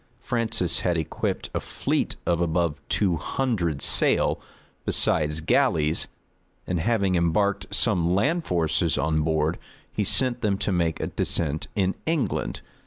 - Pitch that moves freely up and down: No, average, 4.3 semitones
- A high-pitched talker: No, very low, 85 Hz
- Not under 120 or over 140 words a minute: Yes, slow, 135 wpm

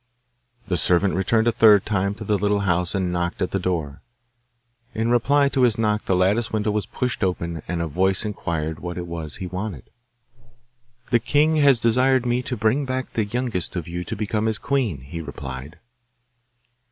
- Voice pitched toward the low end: Yes, low, 100 Hz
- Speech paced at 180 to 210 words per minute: Yes, average, 190 wpm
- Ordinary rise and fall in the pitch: Yes, average, 4.9 semitones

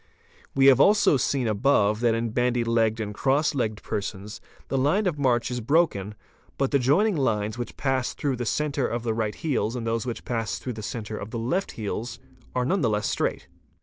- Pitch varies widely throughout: No, average, 3.8 semitones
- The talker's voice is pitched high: No, low, 120 Hz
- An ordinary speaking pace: No, fast, 210 wpm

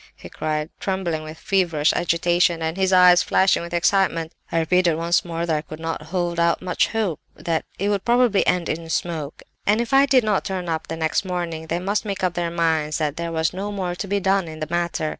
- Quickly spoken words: Yes, fast, 220 wpm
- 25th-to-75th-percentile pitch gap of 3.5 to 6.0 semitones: No, average, 2.7 semitones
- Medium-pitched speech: Yes, medium, 175 Hz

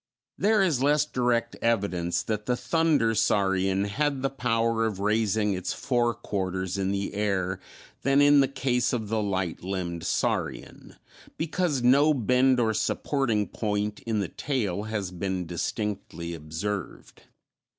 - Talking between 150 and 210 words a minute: No, average, 140 wpm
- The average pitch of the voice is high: No, low, 110 Hz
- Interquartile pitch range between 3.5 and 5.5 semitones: Yes, average, 4.8 semitones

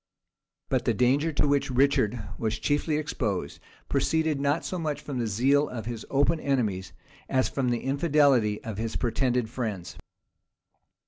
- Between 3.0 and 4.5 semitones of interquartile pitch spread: Yes, average, 4.1 semitones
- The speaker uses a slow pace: No, average, 150 wpm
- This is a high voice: No, low, 130 Hz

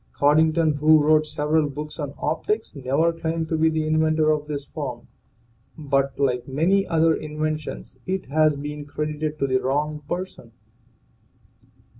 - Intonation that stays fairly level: Yes, narrow, 1.6 semitones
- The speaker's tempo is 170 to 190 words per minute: No, average, 145 wpm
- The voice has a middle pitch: Yes, medium, 155 Hz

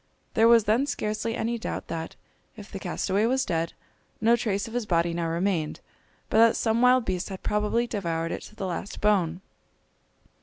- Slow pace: No, average, 185 wpm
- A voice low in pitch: No, high, 210 Hz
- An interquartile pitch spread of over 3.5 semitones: Yes, average, 4.7 semitones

